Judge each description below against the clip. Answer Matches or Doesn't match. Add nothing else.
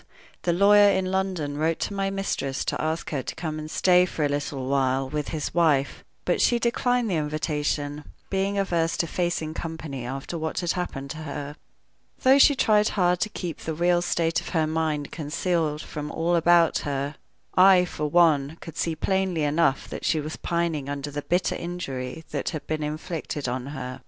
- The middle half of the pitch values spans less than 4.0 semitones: Matches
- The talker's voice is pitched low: Doesn't match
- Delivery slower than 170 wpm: Doesn't match